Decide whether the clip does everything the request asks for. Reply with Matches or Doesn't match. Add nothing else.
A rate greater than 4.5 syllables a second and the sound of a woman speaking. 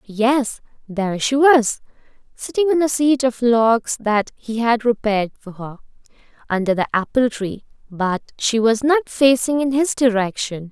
Doesn't match